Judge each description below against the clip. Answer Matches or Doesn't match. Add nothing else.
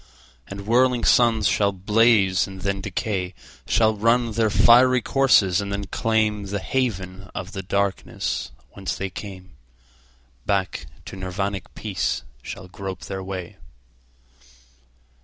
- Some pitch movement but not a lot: Matches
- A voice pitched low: Matches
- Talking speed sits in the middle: Doesn't match